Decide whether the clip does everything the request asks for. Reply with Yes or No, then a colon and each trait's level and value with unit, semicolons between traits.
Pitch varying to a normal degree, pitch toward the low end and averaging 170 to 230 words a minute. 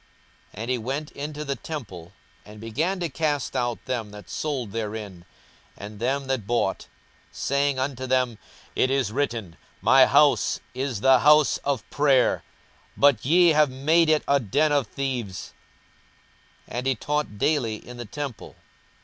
No: average, 4.4 semitones; low, 130 Hz; average, 160 wpm